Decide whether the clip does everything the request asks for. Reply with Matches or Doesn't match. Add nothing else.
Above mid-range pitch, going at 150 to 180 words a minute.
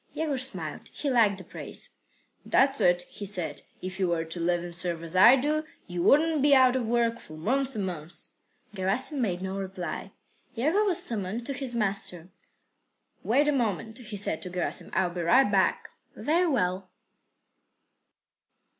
Matches